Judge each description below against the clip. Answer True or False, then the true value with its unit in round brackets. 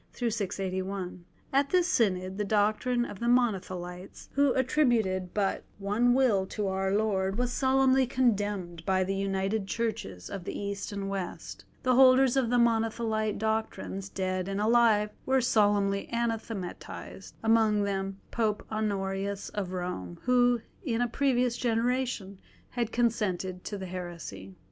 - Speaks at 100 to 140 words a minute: True (135 wpm)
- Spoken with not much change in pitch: False (3.8 semitones)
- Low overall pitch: False (210 Hz)